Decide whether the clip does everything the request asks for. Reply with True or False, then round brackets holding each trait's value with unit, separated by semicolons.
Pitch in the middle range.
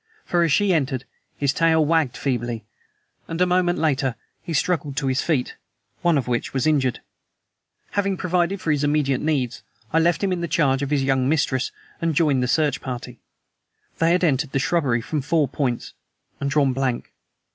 True (145 Hz)